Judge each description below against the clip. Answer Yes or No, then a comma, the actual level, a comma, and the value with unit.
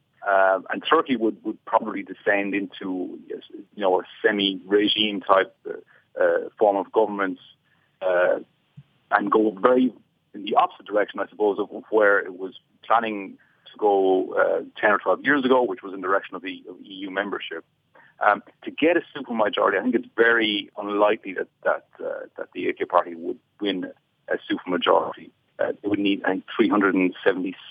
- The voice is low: Yes, low, 130 Hz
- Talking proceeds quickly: No, average, 170 wpm